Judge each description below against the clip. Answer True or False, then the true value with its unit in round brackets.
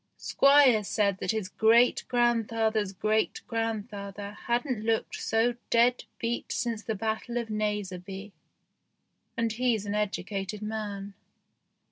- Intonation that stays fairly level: True (2.3 semitones)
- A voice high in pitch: True (220 Hz)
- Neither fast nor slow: False (115 wpm)